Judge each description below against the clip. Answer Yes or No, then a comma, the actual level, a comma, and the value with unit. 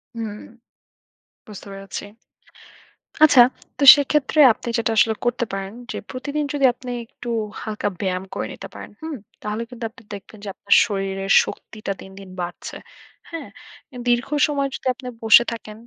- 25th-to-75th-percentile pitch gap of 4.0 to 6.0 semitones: Yes, average, 4.4 semitones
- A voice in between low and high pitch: No, high, 225 Hz